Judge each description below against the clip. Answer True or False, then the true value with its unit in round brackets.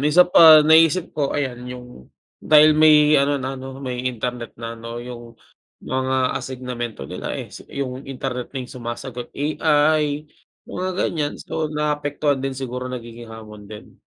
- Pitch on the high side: False (130 Hz)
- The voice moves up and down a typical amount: True (3.6 semitones)